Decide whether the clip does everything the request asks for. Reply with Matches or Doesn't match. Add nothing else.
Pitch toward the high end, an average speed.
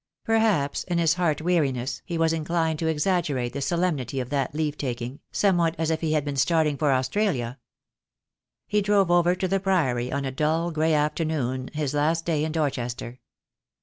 Doesn't match